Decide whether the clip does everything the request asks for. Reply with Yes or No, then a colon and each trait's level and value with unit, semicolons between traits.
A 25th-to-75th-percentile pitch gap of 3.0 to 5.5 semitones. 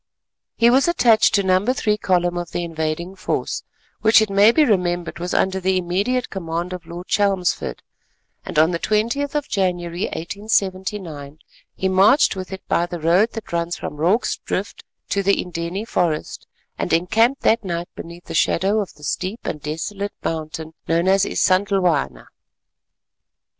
Yes: average, 3.3 semitones